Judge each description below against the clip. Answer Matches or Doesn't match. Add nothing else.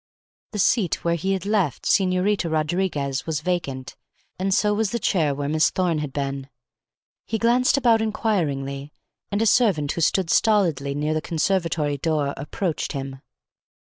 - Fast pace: Doesn't match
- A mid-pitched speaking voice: Matches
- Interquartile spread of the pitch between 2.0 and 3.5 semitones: Doesn't match